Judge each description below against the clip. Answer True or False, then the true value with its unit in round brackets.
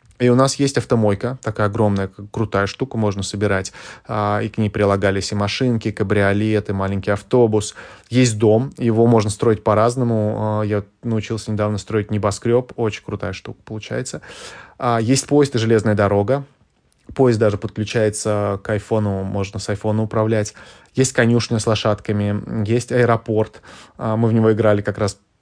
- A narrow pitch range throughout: True (1.9 semitones)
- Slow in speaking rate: False (150 wpm)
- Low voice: True (110 Hz)